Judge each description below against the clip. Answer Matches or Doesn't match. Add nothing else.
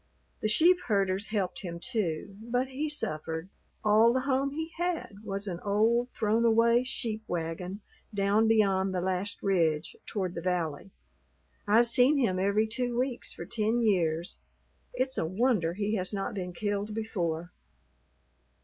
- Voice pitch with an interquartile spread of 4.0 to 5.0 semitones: Matches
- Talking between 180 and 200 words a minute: Doesn't match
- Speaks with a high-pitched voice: Matches